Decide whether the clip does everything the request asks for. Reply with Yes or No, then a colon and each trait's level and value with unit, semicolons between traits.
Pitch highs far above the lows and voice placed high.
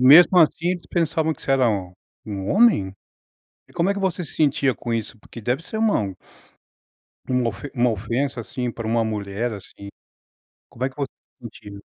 No: wide, 6.7 semitones; low, 125 Hz